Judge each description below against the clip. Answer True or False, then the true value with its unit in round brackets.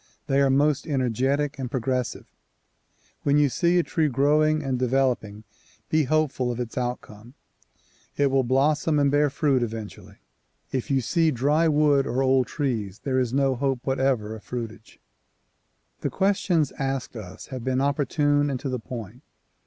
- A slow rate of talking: False (160 wpm)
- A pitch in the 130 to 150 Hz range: True (135 Hz)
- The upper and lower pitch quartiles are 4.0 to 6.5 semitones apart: False (2.7 semitones)